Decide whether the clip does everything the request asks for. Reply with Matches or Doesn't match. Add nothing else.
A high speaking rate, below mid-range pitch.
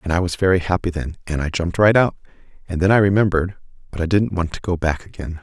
Matches